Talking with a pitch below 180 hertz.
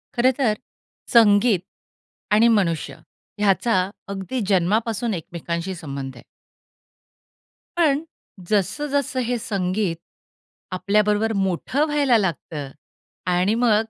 No: high, 210 Hz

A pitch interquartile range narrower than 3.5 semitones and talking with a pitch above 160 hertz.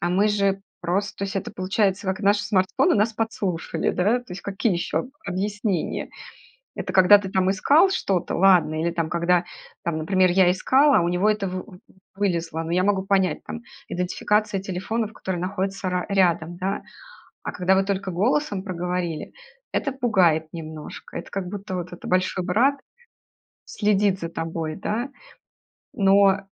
Yes: narrow, 2.4 semitones; high, 190 Hz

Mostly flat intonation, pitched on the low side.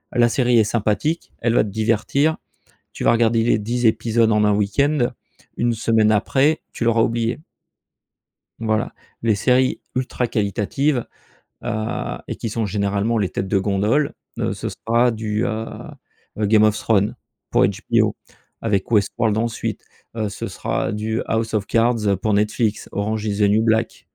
Yes: narrow, 2.0 semitones; low, 110 Hz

